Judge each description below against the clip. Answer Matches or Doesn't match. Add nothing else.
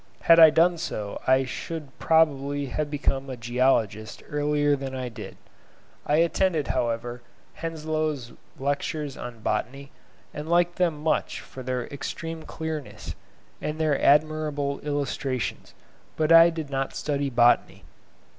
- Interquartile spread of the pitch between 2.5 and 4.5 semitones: Matches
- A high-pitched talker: Doesn't match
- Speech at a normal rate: Doesn't match